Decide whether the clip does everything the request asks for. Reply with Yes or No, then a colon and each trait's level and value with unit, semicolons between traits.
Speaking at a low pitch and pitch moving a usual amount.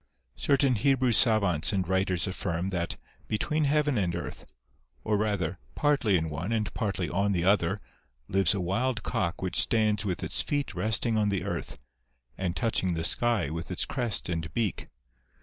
Yes: low, 100 Hz; average, 4.4 semitones